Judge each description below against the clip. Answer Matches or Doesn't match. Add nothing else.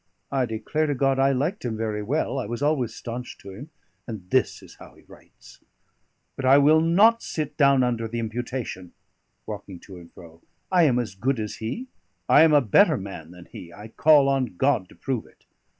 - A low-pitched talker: Matches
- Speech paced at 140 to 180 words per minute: Doesn't match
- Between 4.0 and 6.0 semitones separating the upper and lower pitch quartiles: Matches